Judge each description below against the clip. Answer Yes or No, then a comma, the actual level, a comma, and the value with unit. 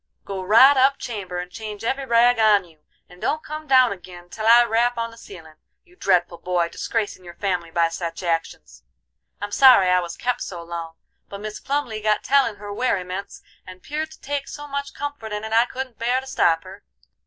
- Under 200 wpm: No, fast, 205 wpm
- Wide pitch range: Yes, wide, 5.9 semitones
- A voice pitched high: Yes, high, 215 Hz